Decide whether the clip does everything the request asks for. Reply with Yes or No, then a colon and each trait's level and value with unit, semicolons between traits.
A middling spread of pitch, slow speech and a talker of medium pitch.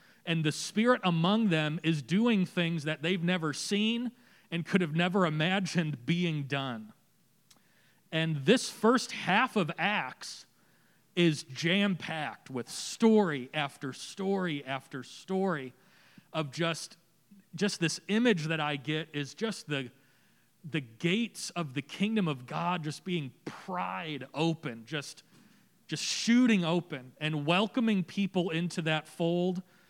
Yes: average, 4.5 semitones; slow, 130 wpm; medium, 170 Hz